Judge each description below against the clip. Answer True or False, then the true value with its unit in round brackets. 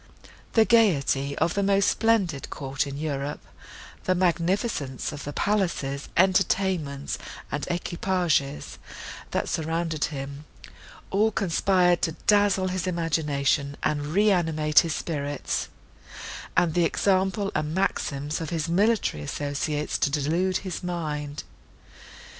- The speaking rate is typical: False (115 wpm)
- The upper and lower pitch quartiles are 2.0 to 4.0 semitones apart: False (4.5 semitones)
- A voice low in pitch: False (165 Hz)